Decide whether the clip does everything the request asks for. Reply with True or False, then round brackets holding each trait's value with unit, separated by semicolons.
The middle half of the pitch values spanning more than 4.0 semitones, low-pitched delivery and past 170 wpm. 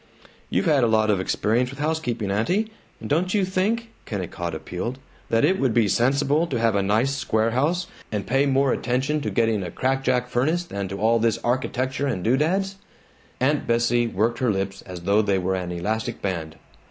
True (5.5 semitones; 120 Hz; 190 wpm)